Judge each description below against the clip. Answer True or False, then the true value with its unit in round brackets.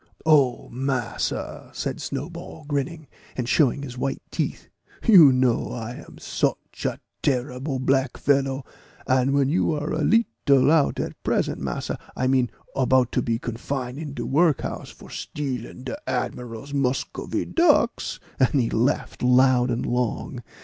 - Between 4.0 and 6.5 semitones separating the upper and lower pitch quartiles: False (2.5 semitones)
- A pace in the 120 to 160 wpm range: True (145 wpm)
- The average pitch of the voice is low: True (130 Hz)